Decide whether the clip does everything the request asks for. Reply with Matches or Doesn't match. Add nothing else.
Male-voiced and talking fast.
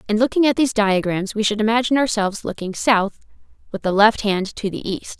Doesn't match